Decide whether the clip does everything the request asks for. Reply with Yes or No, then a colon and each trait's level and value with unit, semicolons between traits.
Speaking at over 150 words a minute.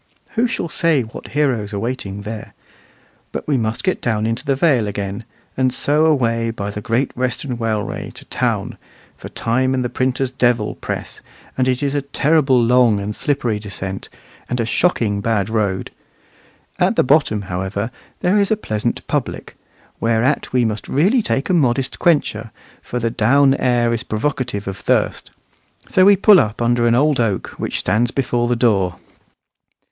Yes: average, 170 wpm